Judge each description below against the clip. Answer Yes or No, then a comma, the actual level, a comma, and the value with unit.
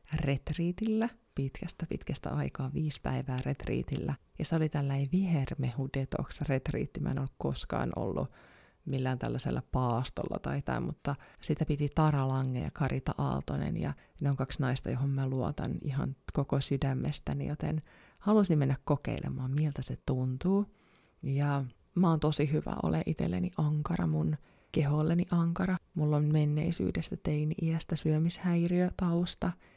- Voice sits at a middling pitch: Yes, medium, 145 Hz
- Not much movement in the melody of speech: No, average, 3.5 semitones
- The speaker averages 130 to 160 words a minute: Yes, average, 135 wpm